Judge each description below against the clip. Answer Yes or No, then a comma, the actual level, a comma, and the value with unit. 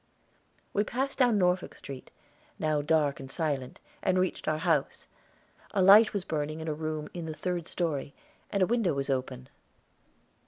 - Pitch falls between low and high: Yes, medium, 160 Hz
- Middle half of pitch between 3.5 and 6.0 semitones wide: Yes, average, 4.1 semitones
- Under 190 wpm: Yes, average, 170 wpm